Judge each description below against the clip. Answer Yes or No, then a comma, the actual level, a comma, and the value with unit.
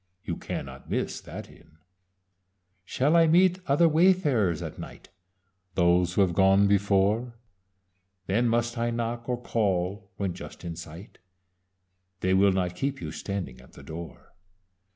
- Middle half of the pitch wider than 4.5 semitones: Yes, average, 5.0 semitones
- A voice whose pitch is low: Yes, low, 100 Hz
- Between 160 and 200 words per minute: No, average, 145 wpm